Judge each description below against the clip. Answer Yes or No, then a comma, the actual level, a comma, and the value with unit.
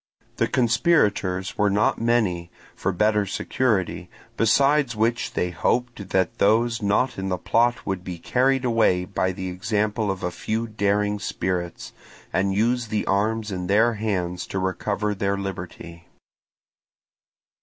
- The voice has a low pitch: Yes, low, 105 Hz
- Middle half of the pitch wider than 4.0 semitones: No, average, 3.5 semitones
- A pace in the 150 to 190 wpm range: No, average, 140 wpm